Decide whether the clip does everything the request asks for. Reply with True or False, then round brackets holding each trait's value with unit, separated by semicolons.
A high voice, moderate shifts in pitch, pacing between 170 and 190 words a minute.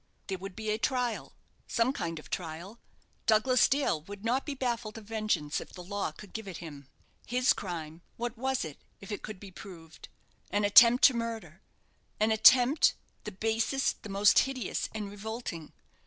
True (215 Hz; 4.3 semitones; 175 wpm)